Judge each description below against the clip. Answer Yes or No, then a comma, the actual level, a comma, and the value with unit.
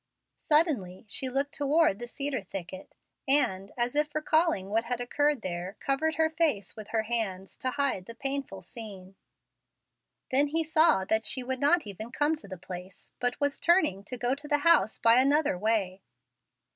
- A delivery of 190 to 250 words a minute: No, average, 175 wpm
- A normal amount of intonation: No, wide, 6.6 semitones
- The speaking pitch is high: Yes, high, 245 Hz